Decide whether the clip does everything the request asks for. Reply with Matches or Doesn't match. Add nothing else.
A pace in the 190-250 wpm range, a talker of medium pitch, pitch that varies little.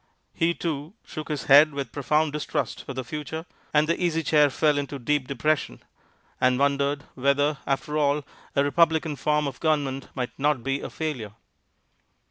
Doesn't match